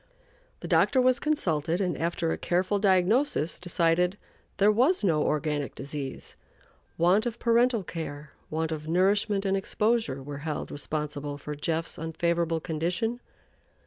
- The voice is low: No, medium, 170 Hz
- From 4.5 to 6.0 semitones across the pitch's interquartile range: Yes, average, 5.1 semitones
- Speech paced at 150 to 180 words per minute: No, slow, 135 wpm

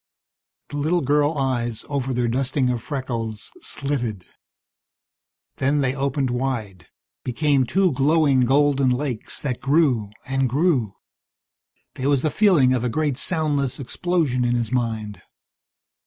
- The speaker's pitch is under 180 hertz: Yes, low, 135 Hz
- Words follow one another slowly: Yes, slow, 130 wpm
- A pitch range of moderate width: Yes, average, 3.0 semitones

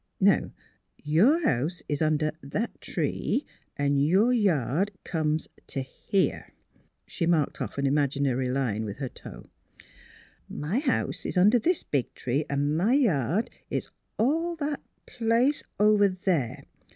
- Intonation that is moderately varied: No, wide, 7.9 semitones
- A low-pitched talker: No, medium, 160 Hz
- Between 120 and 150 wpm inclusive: Yes, average, 140 wpm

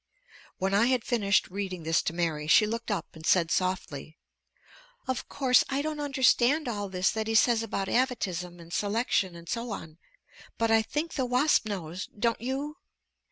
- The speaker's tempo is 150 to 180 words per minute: Yes, average, 175 wpm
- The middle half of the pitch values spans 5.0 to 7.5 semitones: Yes, wide, 5.6 semitones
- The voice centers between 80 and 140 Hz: No, high, 215 Hz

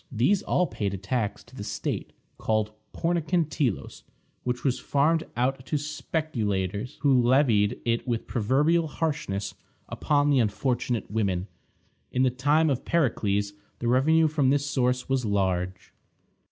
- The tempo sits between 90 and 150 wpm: Yes, average, 140 wpm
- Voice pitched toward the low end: Yes, low, 125 Hz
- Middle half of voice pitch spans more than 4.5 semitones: Yes, wide, 5.6 semitones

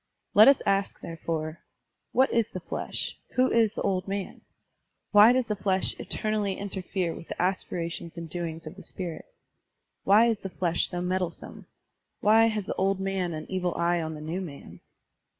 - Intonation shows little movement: No, average, 3.4 semitones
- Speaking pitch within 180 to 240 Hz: Yes, medium, 185 Hz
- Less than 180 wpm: No, average, 190 wpm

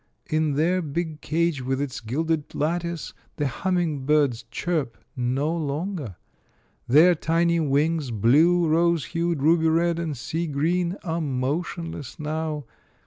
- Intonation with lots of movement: No, average, 3.2 semitones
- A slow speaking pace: Yes, slow, 130 wpm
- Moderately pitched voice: Yes, medium, 160 Hz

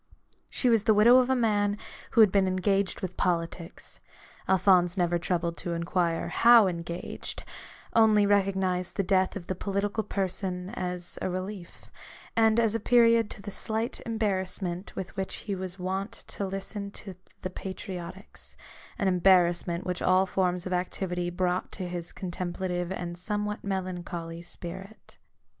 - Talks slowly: No, average, 155 wpm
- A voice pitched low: No, high, 190 Hz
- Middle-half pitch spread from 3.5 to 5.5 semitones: No, narrow, 2.4 semitones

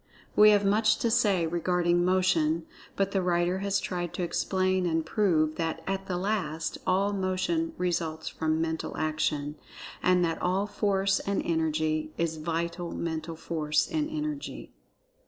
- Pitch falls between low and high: Yes, medium, 175 Hz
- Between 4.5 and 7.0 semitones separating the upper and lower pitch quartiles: No, average, 3.3 semitones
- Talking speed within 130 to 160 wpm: Yes, average, 150 wpm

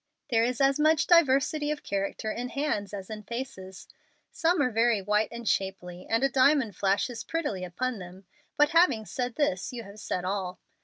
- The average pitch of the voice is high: Yes, high, 230 Hz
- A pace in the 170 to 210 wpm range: Yes, average, 185 wpm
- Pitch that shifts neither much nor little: No, wide, 5.7 semitones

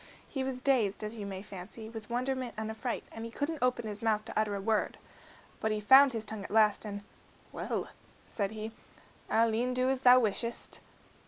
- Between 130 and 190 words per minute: No, average, 200 wpm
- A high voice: Yes, high, 225 Hz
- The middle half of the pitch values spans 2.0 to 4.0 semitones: Yes, average, 2.9 semitones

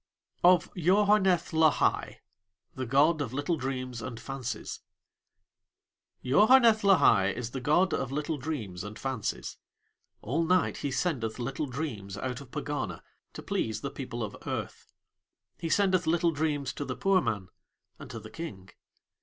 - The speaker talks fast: No, average, 145 wpm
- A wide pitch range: Yes, wide, 5.7 semitones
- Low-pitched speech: No, medium, 145 Hz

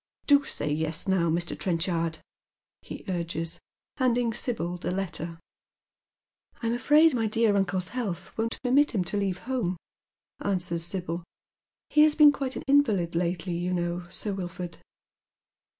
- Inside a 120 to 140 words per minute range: No, average, 150 wpm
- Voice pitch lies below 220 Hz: Yes, medium, 185 Hz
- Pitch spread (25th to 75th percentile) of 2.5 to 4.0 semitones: No, wide, 5.6 semitones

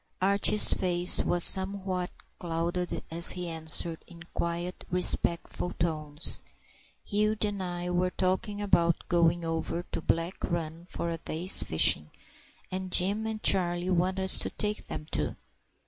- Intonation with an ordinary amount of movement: No, narrow, 1.9 semitones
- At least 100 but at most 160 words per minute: Yes, average, 140 wpm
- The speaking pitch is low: No, medium, 175 Hz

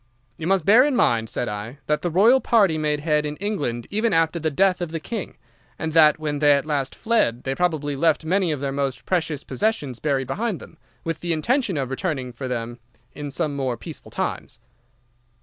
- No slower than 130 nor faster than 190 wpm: No, average, 200 wpm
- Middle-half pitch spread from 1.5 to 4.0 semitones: No, average, 5.1 semitones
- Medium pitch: Yes, medium, 155 Hz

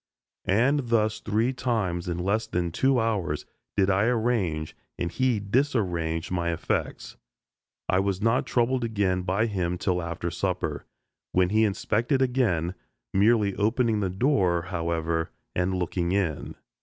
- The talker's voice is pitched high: No, low, 100 Hz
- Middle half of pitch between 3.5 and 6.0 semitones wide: Yes, average, 4.5 semitones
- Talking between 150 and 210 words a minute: No, average, 140 wpm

